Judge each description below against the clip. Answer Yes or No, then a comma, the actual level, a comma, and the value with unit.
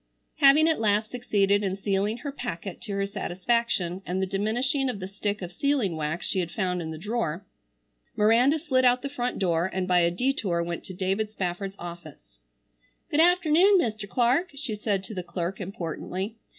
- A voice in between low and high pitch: No, high, 200 Hz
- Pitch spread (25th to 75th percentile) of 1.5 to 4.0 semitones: No, average, 5.3 semitones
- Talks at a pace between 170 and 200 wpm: Yes, average, 185 wpm